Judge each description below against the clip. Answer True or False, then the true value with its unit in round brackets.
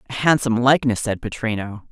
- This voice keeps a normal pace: True (155 wpm)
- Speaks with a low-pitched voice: True (120 Hz)